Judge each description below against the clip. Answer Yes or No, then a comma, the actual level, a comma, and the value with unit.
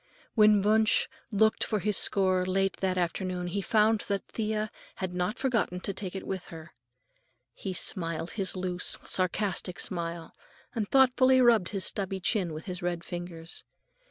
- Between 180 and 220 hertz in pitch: Yes, high, 190 Hz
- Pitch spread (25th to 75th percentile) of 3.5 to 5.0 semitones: No, average, 3.1 semitones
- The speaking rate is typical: Yes, average, 155 wpm